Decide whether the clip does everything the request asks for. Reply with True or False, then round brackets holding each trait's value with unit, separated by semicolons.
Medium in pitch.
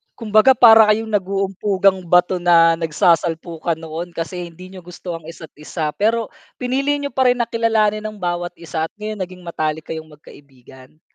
True (180 Hz)